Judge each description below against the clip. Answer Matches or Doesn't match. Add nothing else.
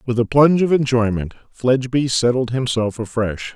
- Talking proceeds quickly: Doesn't match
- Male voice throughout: Matches